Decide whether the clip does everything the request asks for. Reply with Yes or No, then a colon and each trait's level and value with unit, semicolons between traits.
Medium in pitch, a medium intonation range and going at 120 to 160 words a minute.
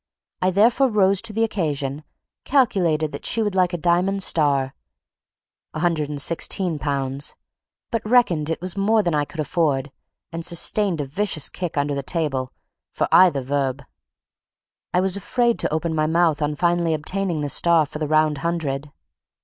Yes: medium, 165 Hz; average, 4.3 semitones; average, 155 wpm